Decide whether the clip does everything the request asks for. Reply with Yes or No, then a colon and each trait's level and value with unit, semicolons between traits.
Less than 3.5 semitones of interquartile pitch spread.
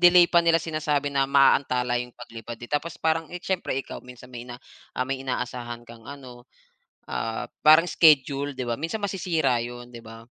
No: average, 4.6 semitones